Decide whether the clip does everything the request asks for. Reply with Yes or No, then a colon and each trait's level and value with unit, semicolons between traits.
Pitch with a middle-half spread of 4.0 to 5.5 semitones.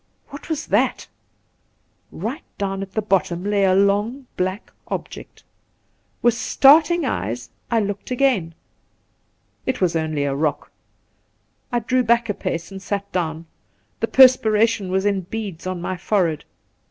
Yes: average, 4.7 semitones